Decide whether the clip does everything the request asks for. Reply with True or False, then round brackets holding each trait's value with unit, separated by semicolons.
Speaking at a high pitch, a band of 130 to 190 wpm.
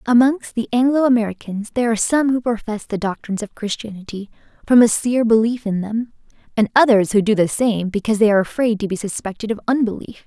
False (220 Hz; 200 wpm)